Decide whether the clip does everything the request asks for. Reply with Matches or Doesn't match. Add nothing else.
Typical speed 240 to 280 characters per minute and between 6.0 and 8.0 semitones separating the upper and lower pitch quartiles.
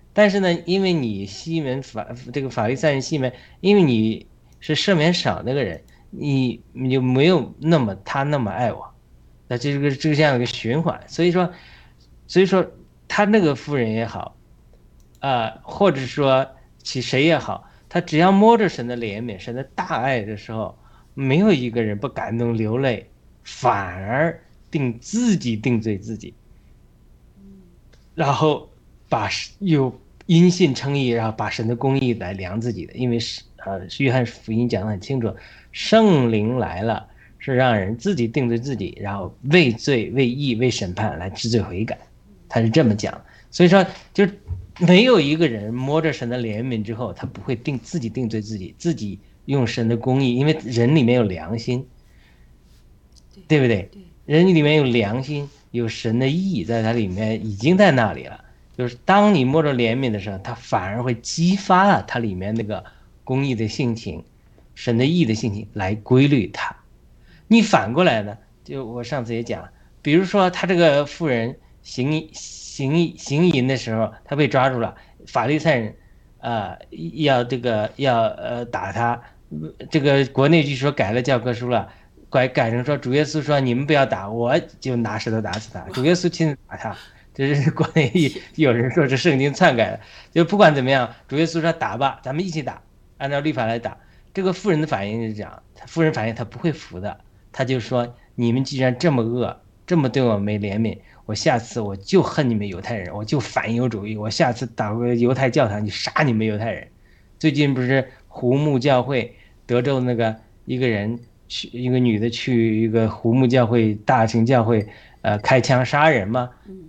Doesn't match